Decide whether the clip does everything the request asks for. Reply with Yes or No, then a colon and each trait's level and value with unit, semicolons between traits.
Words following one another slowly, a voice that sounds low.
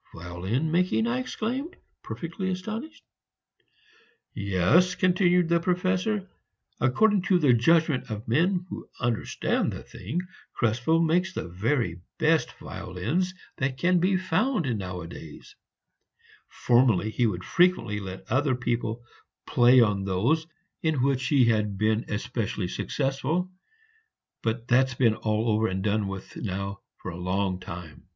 Yes: slow, 130 wpm; low, 125 Hz